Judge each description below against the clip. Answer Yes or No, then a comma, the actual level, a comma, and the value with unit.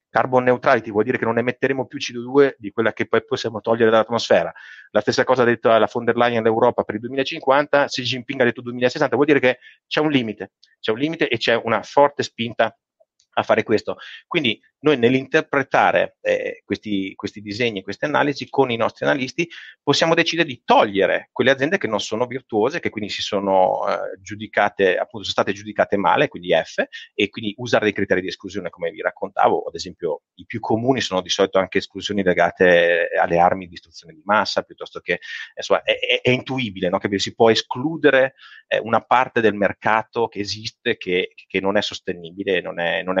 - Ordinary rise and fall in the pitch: No, wide, 5.8 semitones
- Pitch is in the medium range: No, low, 115 Hz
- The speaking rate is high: Yes, fast, 200 wpm